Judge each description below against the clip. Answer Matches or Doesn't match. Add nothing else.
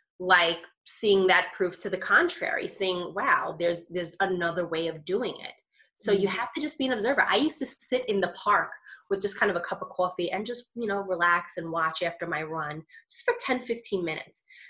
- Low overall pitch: Doesn't match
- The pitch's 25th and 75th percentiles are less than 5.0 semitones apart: Doesn't match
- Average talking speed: Doesn't match